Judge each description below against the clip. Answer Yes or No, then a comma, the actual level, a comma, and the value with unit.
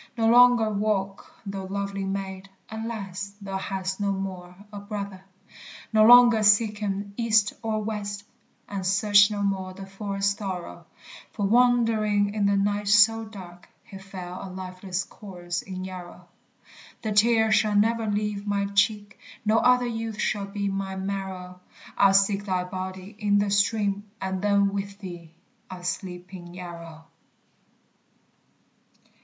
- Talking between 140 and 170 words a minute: Yes, average, 145 wpm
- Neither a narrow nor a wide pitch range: No, narrow, 1.9 semitones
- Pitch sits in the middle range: No, high, 200 Hz